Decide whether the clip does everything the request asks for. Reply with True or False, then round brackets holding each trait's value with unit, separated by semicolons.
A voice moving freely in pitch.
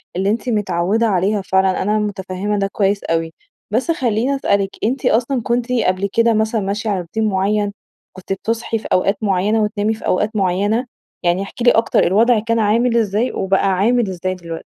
False (3.1 semitones)